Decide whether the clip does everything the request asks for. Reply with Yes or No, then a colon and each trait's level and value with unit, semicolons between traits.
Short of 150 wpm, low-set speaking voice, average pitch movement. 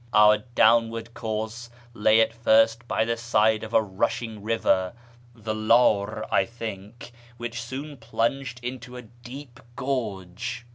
No: slow, 135 wpm; low, 115 Hz; narrow, 1.7 semitones